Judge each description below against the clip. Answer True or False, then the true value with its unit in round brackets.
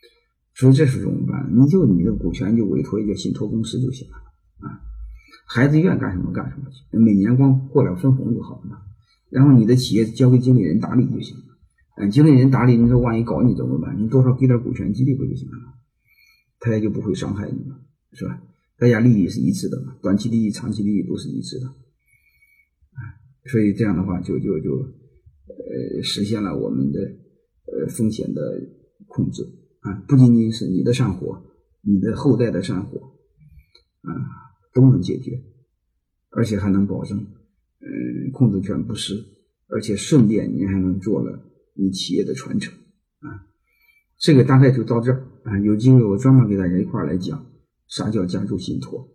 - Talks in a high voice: False (115 Hz)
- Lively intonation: False (4.6 semitones)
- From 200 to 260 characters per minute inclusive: False (275 characters per minute)